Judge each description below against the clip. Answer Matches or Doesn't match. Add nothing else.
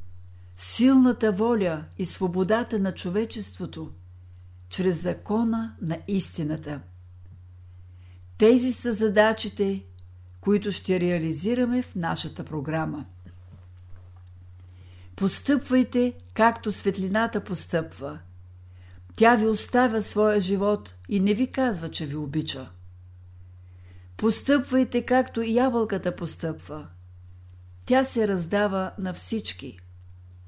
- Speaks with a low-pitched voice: Doesn't match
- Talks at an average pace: Doesn't match